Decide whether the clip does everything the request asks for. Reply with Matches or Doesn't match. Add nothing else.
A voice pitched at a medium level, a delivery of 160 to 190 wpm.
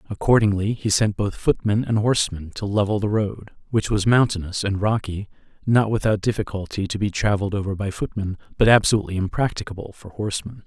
Doesn't match